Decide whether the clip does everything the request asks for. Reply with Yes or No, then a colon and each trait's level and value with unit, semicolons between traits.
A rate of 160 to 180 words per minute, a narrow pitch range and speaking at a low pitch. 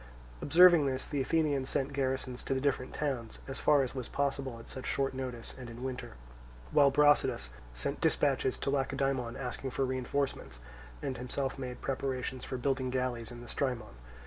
Yes: average, 170 wpm; narrow, 1.7 semitones; low, 130 Hz